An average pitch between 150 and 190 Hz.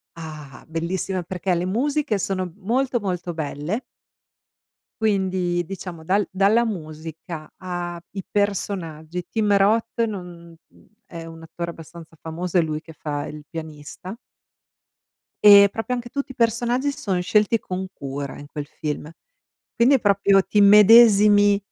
Yes: medium, 185 Hz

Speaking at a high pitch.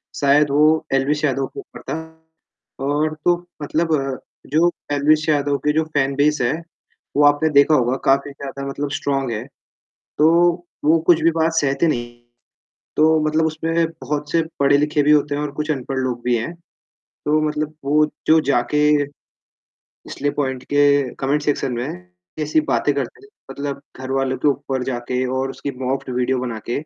No: medium, 145 Hz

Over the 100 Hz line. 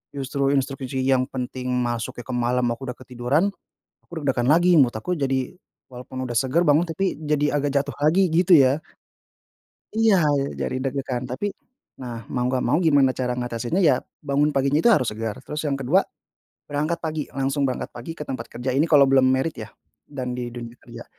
Yes: low, 135 Hz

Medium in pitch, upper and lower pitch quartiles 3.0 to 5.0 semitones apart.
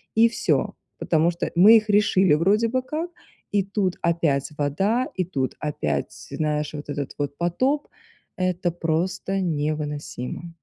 No: medium, 175 Hz; wide, 5.4 semitones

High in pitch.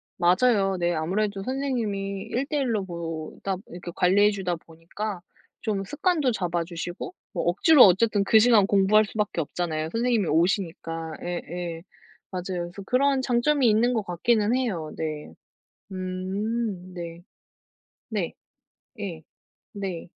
Yes: high, 195 Hz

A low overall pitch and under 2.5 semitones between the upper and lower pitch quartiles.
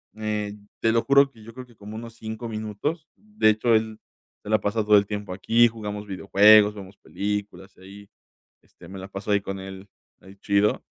Yes: low, 105 Hz; narrow, 1.9 semitones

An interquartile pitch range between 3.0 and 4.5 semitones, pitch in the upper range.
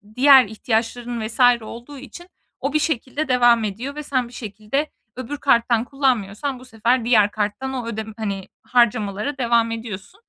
Yes: average, 3.3 semitones; high, 240 Hz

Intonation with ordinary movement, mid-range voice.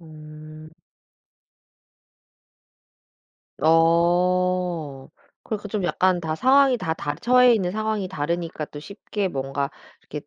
Yes: average, 4.4 semitones; medium, 170 Hz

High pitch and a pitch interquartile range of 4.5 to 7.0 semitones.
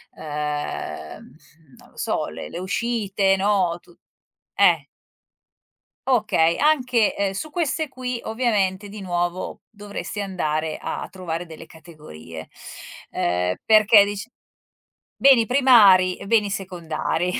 Yes: high, 195 Hz; average, 4.9 semitones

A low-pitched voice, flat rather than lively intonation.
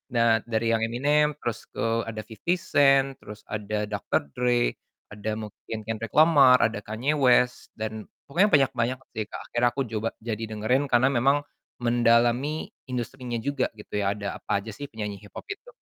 No: low, 120 Hz; average, 3.6 semitones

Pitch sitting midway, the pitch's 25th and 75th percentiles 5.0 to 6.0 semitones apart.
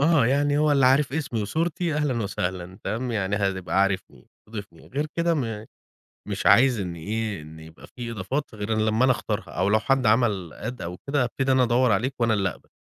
No: low, 115 Hz; wide, 5.4 semitones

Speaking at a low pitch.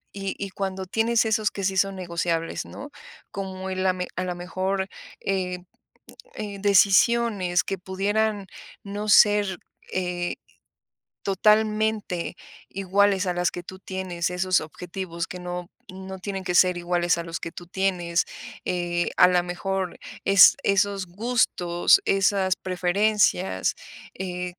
No: high, 190 Hz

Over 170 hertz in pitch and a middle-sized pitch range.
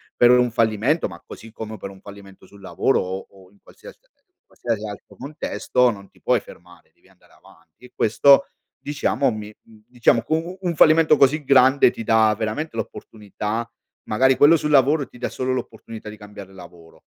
No: low, 115 Hz; average, 4.9 semitones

